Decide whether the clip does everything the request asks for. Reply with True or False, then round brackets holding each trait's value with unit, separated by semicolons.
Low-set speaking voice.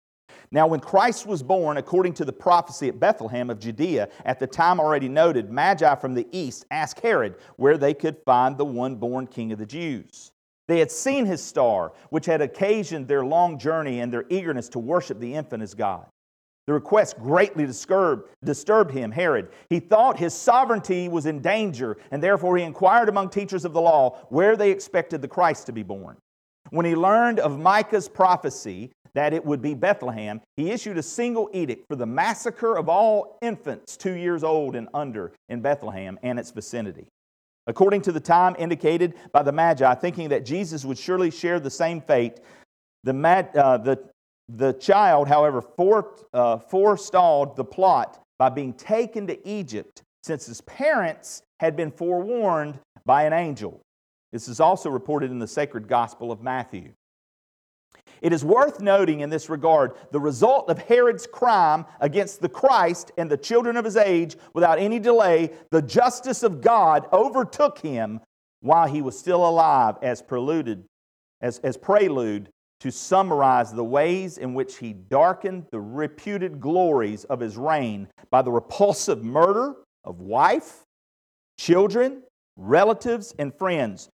False (160 Hz)